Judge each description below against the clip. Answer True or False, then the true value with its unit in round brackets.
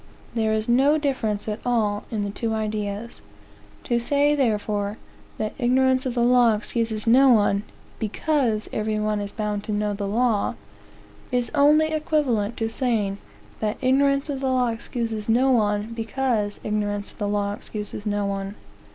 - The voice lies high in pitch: True (225 Hz)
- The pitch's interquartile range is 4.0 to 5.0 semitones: False (3.4 semitones)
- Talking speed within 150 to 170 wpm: True (160 wpm)